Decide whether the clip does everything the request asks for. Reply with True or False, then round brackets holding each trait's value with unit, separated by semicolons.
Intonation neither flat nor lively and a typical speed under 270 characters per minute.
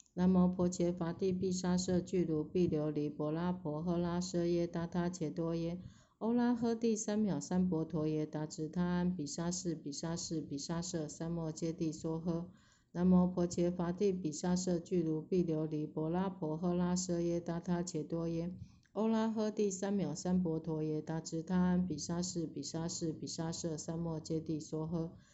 False (2.1 semitones; 260 characters per minute)